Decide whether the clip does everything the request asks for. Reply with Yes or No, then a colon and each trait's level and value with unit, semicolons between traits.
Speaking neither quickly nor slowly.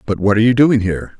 No: fast, 300 wpm